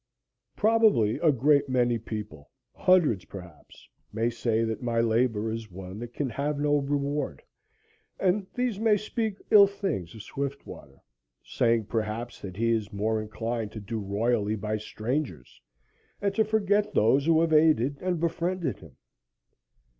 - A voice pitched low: Yes, low, 120 Hz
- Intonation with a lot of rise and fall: Yes, wide, 7.2 semitones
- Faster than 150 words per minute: No, average, 145 wpm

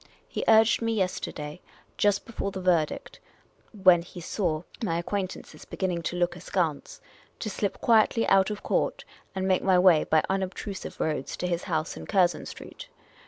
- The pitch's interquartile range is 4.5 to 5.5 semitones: No, average, 2.8 semitones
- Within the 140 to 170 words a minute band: Yes, average, 165 wpm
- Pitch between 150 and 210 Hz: Yes, medium, 185 Hz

